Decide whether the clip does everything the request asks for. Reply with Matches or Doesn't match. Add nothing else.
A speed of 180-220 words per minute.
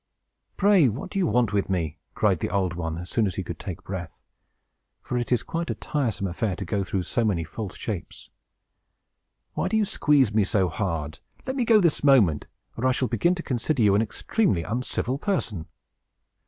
Matches